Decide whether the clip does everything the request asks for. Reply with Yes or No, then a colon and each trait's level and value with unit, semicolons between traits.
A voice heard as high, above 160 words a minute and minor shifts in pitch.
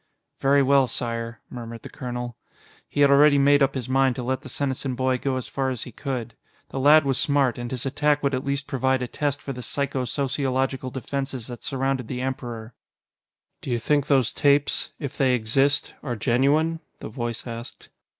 No: low, 130 Hz; average, 195 wpm; narrow, 2.2 semitones